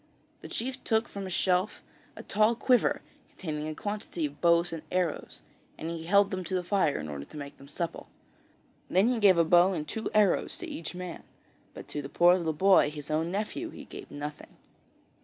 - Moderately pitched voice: Yes, medium, 175 Hz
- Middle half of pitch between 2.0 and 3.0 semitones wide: No, average, 4.4 semitones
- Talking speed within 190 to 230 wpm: Yes, fast, 205 wpm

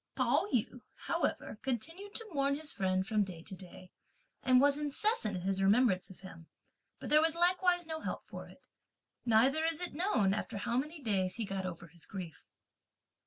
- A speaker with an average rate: Yes, average, 185 wpm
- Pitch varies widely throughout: Yes, wide, 8.6 semitones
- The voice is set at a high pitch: Yes, high, 235 Hz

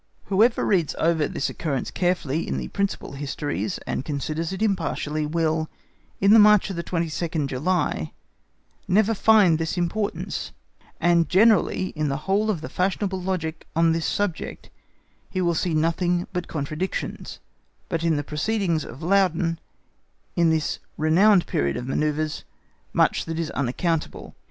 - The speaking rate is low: No, average, 145 wpm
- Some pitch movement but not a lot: Yes, average, 3.5 semitones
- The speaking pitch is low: No, medium, 170 Hz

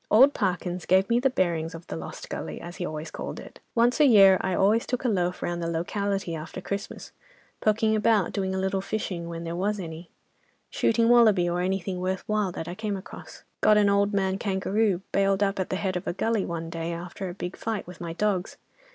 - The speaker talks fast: Yes, fast, 220 wpm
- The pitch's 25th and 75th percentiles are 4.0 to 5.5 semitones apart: No, average, 3.1 semitones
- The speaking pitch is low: No, high, 190 Hz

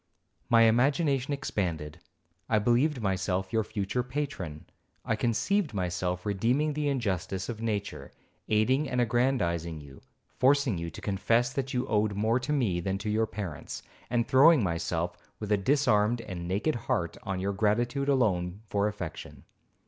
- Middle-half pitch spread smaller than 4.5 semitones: No, average, 5.2 semitones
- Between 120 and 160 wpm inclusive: Yes, average, 150 wpm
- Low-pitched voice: Yes, low, 110 Hz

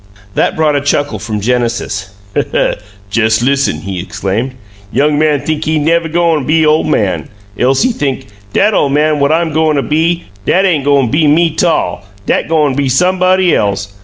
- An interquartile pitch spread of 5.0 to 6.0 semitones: No, average, 4.6 semitones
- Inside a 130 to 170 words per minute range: No, average, 185 wpm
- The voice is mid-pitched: Yes, medium, 145 Hz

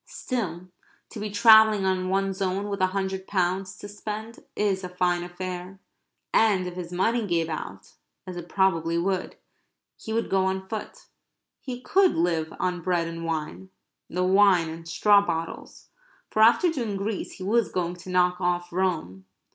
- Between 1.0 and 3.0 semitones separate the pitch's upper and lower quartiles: Yes, average, 2.7 semitones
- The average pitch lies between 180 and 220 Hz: Yes, medium, 185 Hz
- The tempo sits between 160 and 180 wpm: Yes, average, 170 wpm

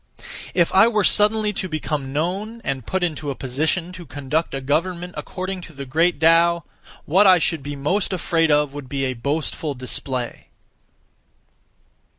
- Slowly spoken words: No, average, 165 wpm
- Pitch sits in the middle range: Yes, medium, 160 Hz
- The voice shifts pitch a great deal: No, average, 4.6 semitones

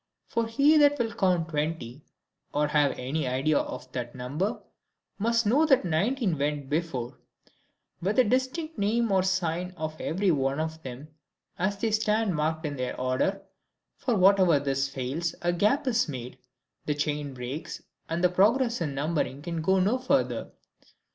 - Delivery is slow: No, average, 160 wpm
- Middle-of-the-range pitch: Yes, medium, 170 Hz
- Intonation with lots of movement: Yes, wide, 6.7 semitones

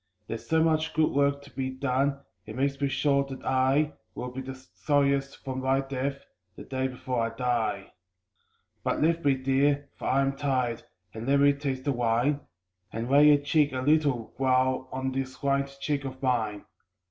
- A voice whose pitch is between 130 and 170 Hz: Yes, low, 135 Hz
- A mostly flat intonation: Yes, narrow, 1.6 semitones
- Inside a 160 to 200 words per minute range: Yes, average, 185 wpm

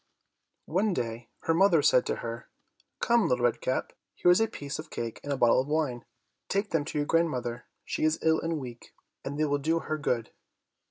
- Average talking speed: No, fast, 210 wpm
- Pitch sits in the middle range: Yes, medium, 145 Hz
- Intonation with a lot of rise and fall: No, average, 5.0 semitones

